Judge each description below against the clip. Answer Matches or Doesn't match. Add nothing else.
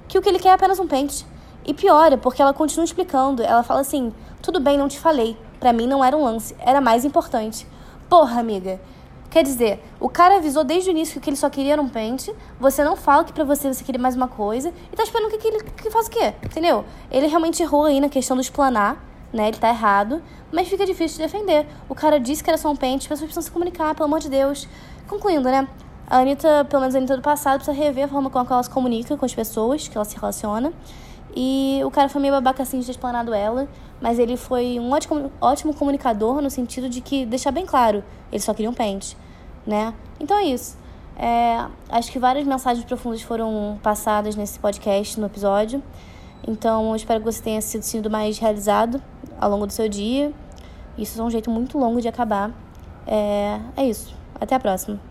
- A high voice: Matches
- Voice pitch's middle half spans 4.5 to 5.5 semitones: Matches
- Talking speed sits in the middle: Doesn't match